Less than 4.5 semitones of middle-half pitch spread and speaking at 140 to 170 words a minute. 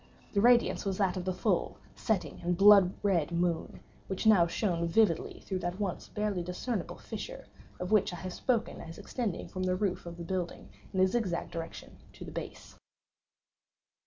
No: average, 3.0 semitones; average, 185 wpm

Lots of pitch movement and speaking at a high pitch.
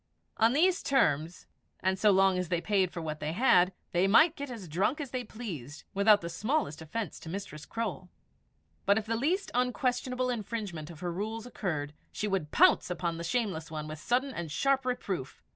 Yes: wide, 6.5 semitones; high, 195 Hz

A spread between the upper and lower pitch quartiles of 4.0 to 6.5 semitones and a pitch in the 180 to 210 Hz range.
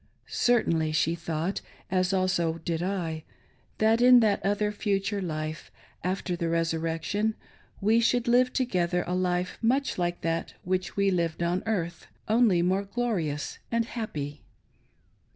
Yes: average, 4.4 semitones; medium, 185 Hz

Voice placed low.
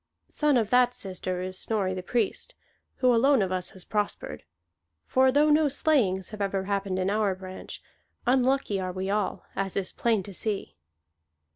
No: high, 205 Hz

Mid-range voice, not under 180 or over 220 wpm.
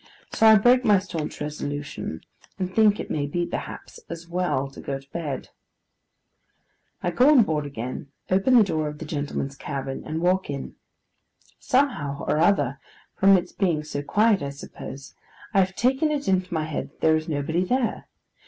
No: medium, 170 Hz; average, 170 wpm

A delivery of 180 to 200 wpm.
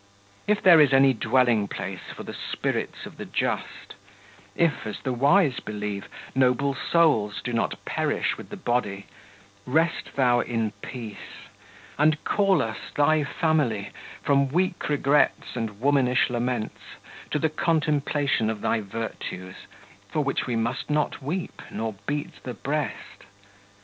No: average, 145 wpm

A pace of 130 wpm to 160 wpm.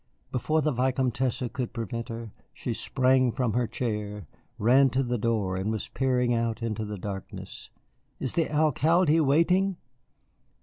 Yes: average, 145 wpm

